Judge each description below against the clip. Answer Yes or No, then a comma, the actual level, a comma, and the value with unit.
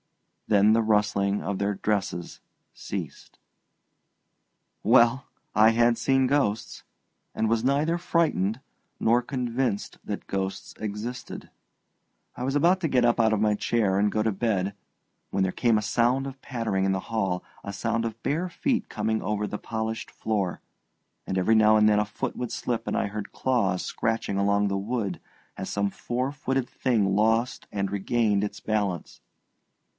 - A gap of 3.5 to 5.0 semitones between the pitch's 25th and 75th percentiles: No, average, 3.1 semitones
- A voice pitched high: No, low, 110 Hz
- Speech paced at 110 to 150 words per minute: No, average, 165 wpm